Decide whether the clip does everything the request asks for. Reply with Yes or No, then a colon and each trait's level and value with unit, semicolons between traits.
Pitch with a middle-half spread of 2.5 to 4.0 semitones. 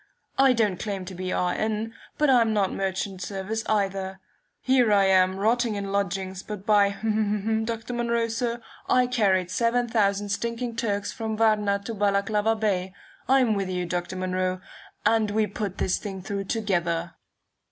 Yes: average, 2.9 semitones